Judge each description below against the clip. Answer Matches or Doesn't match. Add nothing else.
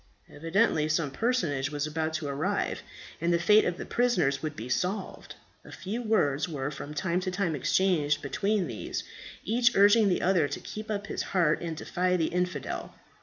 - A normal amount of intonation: Matches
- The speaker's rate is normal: Matches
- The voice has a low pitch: Doesn't match